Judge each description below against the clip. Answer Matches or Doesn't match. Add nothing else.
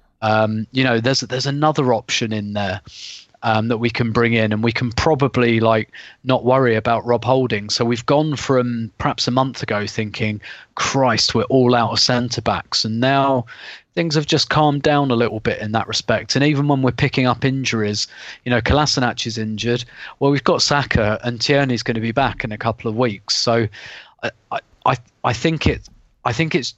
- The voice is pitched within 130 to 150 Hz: Doesn't match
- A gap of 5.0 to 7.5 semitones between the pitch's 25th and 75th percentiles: Doesn't match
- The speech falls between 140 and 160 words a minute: Doesn't match